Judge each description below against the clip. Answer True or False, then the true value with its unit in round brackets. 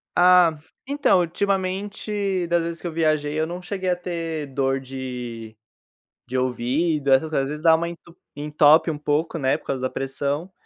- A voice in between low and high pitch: True (160 Hz)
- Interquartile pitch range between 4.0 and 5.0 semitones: True (4.5 semitones)